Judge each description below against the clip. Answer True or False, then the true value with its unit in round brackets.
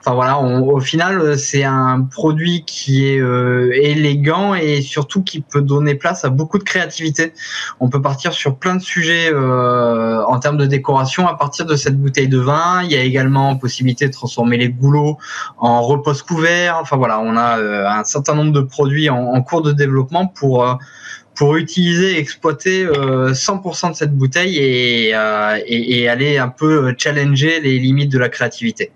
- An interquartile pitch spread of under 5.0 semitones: True (3.6 semitones)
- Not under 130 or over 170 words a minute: False (185 wpm)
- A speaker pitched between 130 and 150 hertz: True (140 Hz)